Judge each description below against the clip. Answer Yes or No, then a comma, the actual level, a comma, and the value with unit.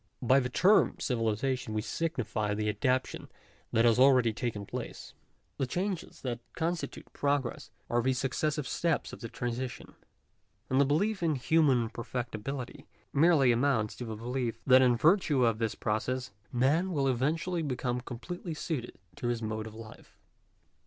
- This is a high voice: No, low, 125 Hz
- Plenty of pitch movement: No, average, 3.9 semitones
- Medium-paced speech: Yes, average, 160 wpm